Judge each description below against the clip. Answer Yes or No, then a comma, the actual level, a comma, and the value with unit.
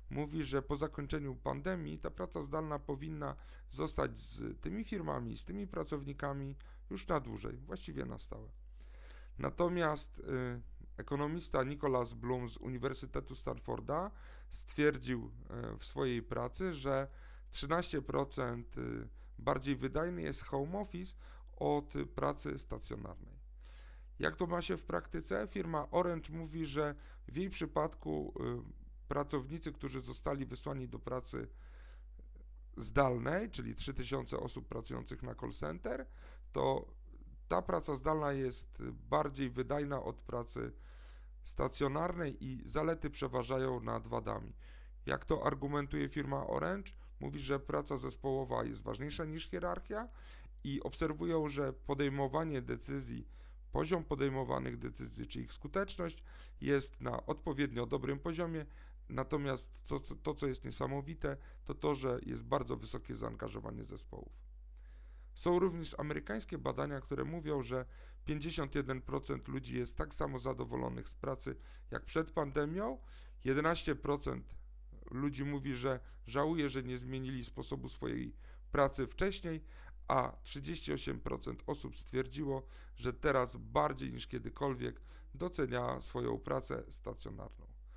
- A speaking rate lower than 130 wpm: Yes, average, 120 wpm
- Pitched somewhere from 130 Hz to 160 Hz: Yes, low, 135 Hz